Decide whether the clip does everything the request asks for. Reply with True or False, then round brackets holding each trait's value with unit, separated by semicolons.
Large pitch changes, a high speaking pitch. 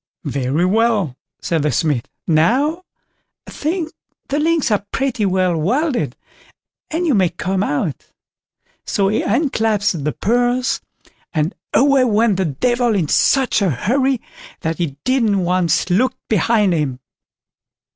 True (7.0 semitones; 205 Hz)